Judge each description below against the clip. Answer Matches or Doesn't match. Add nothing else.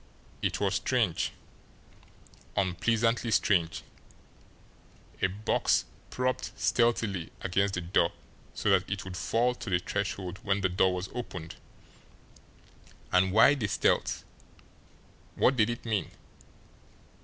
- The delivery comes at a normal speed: Doesn't match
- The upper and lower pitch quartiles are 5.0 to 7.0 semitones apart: Doesn't match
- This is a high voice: Doesn't match